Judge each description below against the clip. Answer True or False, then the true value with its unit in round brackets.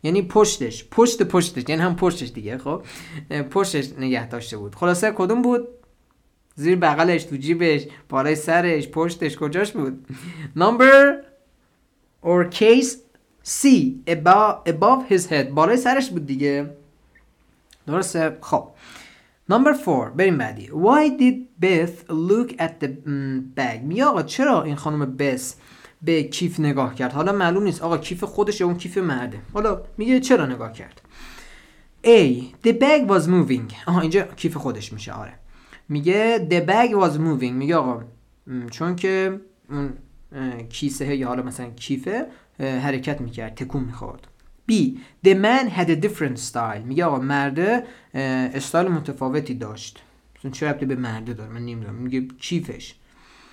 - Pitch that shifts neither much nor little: False (6.6 semitones)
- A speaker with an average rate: True (140 wpm)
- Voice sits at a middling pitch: True (160 Hz)